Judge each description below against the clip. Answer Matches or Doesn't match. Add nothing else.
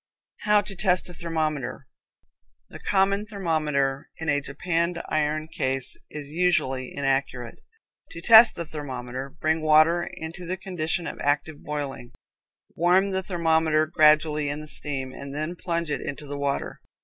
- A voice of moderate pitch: Matches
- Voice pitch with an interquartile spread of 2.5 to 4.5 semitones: Matches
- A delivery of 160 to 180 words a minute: Doesn't match